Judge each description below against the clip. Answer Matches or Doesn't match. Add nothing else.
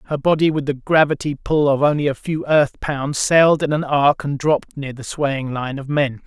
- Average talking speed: Doesn't match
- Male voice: Matches